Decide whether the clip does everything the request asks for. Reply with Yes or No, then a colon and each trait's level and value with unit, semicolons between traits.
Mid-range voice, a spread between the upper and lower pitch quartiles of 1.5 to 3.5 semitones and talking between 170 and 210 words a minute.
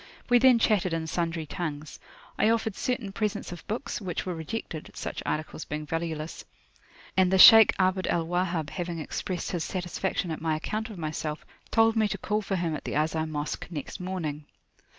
No: medium, 175 Hz; average, 3.9 semitones; average, 185 wpm